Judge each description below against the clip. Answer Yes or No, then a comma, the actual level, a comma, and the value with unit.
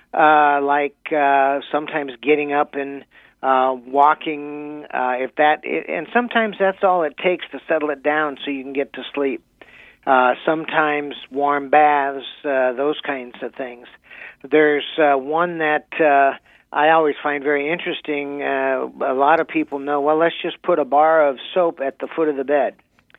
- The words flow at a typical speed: Yes, average, 175 wpm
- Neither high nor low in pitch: Yes, medium, 145 Hz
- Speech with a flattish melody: Yes, narrow, 2.1 semitones